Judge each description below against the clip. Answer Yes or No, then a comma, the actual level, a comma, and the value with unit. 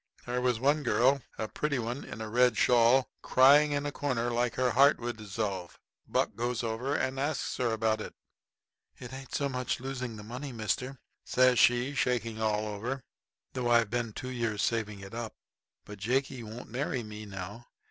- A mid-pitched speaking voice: No, low, 120 Hz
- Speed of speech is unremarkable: Yes, average, 185 wpm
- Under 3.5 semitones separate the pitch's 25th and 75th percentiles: Yes, average, 2.8 semitones